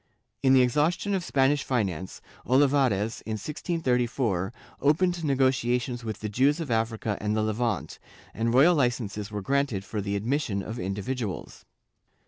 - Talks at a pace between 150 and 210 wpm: No, average, 140 wpm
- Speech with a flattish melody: No, average, 4.8 semitones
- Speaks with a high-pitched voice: No, low, 120 Hz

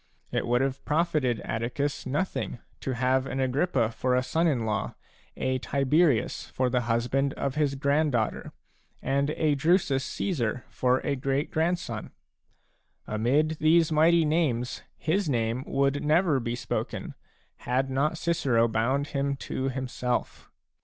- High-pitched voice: No, low, 135 Hz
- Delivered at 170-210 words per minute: No, average, 140 wpm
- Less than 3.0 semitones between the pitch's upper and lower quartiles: No, average, 3.6 semitones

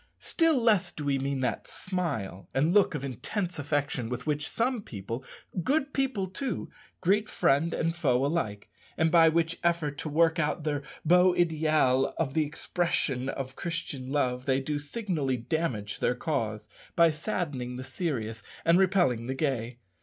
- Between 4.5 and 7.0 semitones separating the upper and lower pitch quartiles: Yes, average, 4.8 semitones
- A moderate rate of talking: Yes, average, 160 wpm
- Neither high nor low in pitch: Yes, medium, 150 Hz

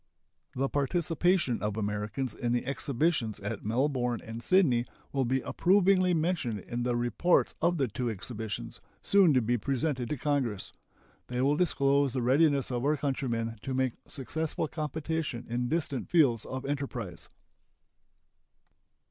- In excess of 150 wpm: No, average, 140 wpm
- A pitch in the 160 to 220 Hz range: No, low, 130 Hz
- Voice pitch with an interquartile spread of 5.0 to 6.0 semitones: No, average, 4.3 semitones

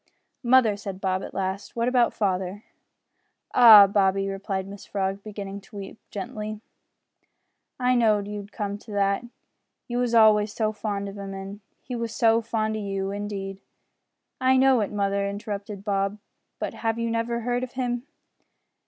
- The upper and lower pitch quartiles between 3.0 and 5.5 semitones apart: No, narrow, 2.6 semitones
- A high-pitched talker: Yes, high, 205 Hz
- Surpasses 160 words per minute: Yes, average, 170 wpm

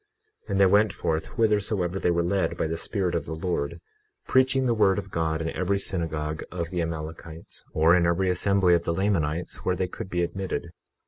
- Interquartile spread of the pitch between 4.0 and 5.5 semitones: No, average, 3.0 semitones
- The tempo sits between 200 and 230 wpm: Yes, fast, 205 wpm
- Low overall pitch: Yes, very low, 90 Hz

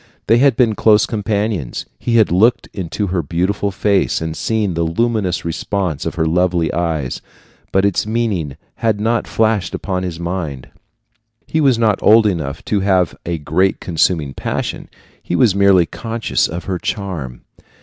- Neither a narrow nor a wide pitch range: Yes, average, 4.5 semitones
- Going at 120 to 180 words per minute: Yes, average, 160 wpm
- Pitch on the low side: Yes, very low, 95 Hz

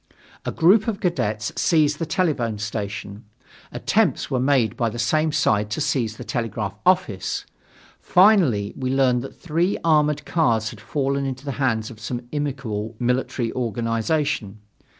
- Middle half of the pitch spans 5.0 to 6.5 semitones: Yes, average, 5.3 semitones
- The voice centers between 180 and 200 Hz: No, low, 125 Hz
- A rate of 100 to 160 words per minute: Yes, average, 150 wpm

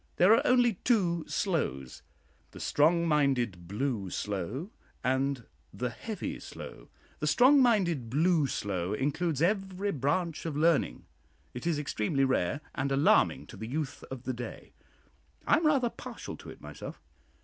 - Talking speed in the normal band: Yes, average, 150 wpm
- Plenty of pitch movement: Yes, wide, 6.2 semitones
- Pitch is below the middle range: No, medium, 145 Hz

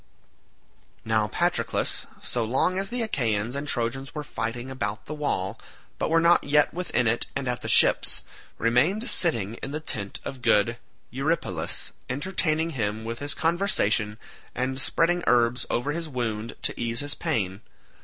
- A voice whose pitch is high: No, low, 130 Hz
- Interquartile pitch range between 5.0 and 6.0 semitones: Yes, wide, 5.4 semitones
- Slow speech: No, average, 155 wpm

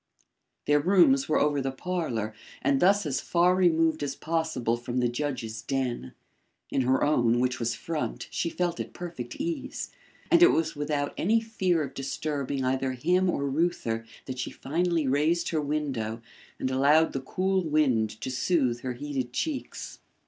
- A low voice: No, medium, 145 Hz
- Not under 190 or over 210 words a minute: No, average, 165 wpm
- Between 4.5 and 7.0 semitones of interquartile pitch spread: Yes, average, 4.8 semitones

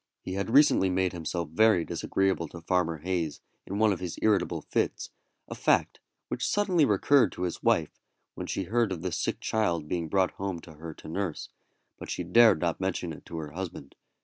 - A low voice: Yes, very low, 90 Hz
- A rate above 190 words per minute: Yes, average, 200 wpm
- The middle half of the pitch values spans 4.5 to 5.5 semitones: No, average, 3.3 semitones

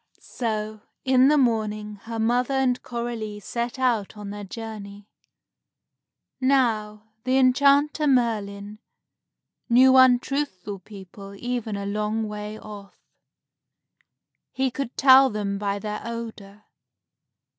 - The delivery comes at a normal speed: No, slow, 110 wpm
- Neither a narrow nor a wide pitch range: Yes, average, 3.5 semitones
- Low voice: No, high, 220 Hz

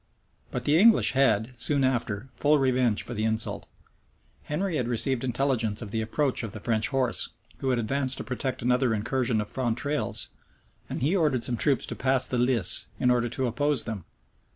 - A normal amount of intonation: Yes, average, 3.0 semitones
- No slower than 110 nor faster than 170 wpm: No, average, 190 wpm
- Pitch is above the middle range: No, low, 125 Hz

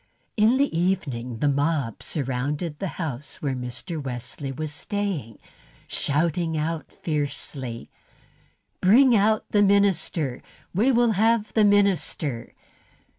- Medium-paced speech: No, slow, 115 wpm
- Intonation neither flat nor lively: No, wide, 6.8 semitones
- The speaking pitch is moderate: Yes, medium, 160 Hz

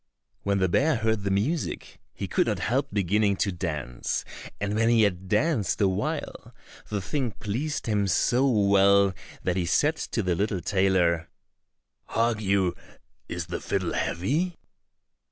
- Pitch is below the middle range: Yes, low, 100 Hz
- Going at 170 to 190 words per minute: No, average, 155 wpm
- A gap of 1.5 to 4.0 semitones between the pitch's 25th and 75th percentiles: Yes, average, 3.5 semitones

